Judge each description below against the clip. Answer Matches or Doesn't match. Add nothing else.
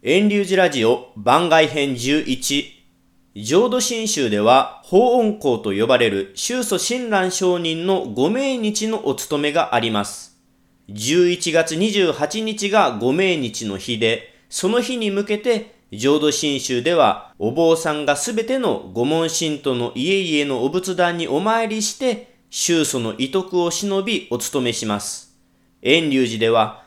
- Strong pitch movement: Matches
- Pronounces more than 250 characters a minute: Doesn't match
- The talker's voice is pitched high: Doesn't match